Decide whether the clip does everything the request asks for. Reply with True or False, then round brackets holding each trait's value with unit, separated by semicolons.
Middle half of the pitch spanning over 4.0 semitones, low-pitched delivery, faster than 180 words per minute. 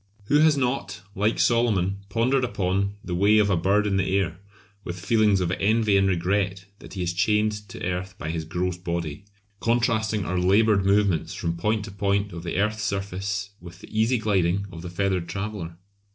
False (2.8 semitones; 100 Hz; 190 wpm)